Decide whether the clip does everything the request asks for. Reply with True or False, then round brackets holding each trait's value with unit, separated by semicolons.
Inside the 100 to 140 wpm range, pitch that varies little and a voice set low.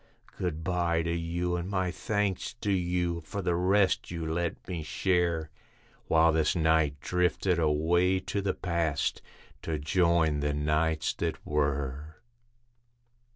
True (135 wpm; 2.2 semitones; 85 Hz)